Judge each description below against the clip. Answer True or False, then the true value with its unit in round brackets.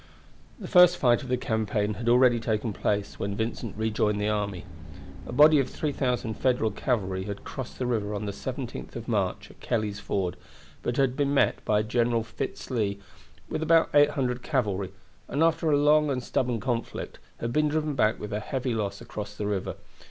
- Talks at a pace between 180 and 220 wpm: True (185 wpm)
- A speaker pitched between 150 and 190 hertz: False (115 Hz)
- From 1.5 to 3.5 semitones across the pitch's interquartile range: False (4.1 semitones)